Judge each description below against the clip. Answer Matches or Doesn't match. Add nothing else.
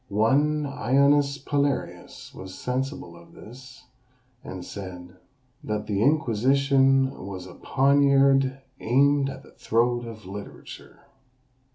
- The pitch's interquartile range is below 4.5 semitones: Doesn't match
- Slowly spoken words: Matches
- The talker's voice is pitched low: Matches